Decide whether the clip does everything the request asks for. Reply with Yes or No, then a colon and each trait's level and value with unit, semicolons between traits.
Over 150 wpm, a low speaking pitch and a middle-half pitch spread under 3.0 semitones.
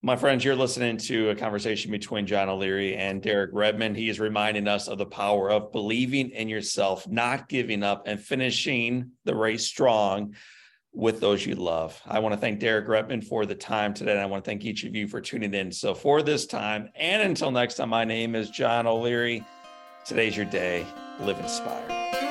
Yes: average, 200 wpm; low, 110 Hz; narrow, 2.6 semitones